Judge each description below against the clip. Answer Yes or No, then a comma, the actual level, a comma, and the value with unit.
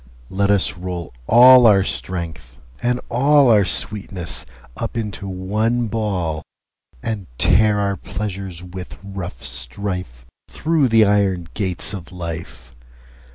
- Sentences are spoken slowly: Yes, slow, 110 wpm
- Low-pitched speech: Yes, very low, 95 Hz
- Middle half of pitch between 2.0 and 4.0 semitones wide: Yes, average, 3.6 semitones